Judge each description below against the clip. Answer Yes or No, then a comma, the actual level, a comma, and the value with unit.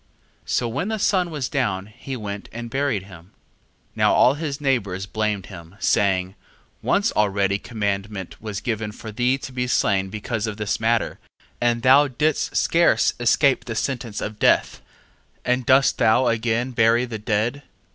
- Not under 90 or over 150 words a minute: No, average, 165 wpm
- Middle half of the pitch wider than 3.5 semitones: Yes, average, 4.0 semitones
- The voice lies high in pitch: No, low, 115 Hz